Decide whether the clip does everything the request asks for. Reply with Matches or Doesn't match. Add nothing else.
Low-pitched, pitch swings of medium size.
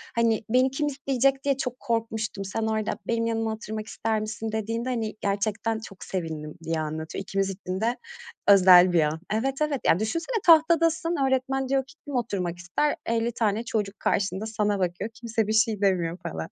Doesn't match